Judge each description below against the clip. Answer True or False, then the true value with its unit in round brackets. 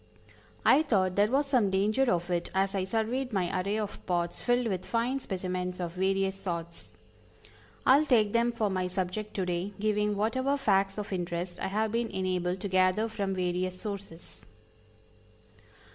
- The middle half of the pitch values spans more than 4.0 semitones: False (3.2 semitones)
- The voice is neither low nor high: False (195 Hz)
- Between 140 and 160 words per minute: False (170 wpm)